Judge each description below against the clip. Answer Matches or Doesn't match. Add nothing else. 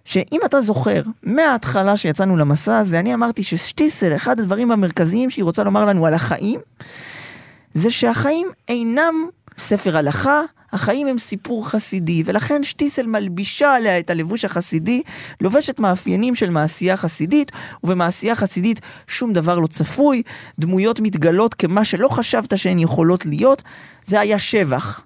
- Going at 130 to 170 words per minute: Matches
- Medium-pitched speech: Doesn't match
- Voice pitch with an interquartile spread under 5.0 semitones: Doesn't match